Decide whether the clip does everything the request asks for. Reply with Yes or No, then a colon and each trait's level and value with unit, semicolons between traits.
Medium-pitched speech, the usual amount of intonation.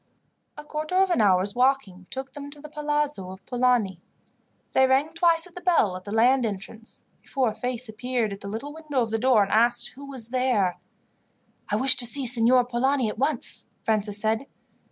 No: very high, 250 Hz; average, 4.4 semitones